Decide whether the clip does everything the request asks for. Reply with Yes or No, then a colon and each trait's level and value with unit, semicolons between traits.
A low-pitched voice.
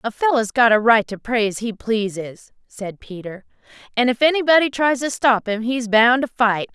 No: high, 230 Hz